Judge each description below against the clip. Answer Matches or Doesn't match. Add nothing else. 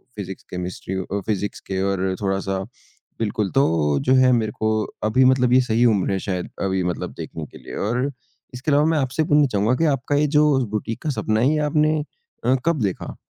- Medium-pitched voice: Doesn't match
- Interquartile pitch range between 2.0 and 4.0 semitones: Doesn't match